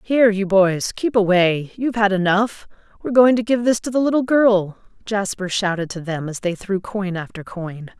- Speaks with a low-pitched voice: No, high, 200 Hz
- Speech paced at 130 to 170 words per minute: No, fast, 205 wpm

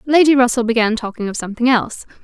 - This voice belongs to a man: No, female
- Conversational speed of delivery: Yes, average, 190 wpm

